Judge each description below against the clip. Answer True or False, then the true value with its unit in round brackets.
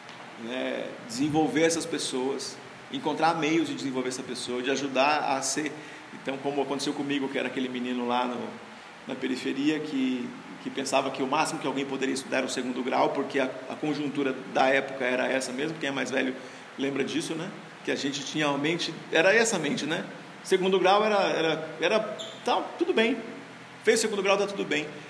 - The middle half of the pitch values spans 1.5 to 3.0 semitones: False (3.5 semitones)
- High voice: False (150 Hz)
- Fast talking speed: True (195 wpm)